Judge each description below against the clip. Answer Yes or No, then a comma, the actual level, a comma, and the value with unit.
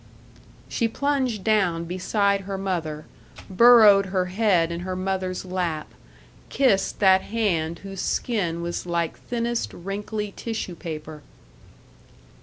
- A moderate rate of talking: No, slow, 115 wpm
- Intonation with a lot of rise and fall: No, average, 3.7 semitones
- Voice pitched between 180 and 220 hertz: Yes, high, 190 Hz